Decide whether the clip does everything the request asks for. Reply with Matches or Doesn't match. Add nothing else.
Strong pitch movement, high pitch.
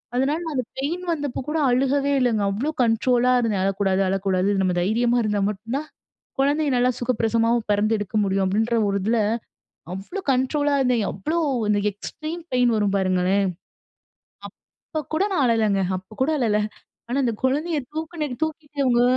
Matches